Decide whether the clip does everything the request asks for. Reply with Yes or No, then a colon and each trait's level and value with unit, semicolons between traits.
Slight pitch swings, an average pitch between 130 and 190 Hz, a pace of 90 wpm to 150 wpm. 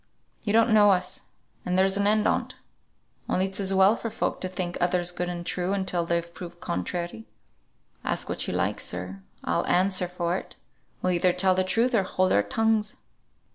No: narrow, 2.2 semitones; medium, 185 Hz; average, 185 wpm